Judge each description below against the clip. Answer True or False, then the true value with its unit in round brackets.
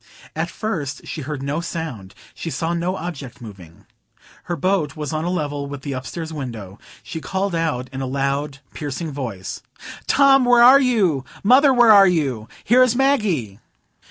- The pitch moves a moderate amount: False (6.4 semitones)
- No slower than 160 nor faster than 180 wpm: True (170 wpm)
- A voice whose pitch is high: False (155 Hz)